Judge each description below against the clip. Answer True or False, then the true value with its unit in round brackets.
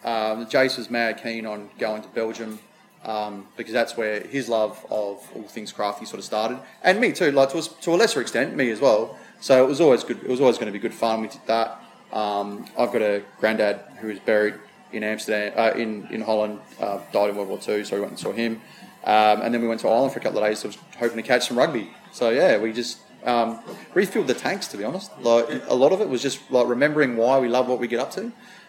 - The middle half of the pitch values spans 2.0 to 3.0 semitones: True (2.4 semitones)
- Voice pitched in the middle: False (115 Hz)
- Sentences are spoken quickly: True (260 wpm)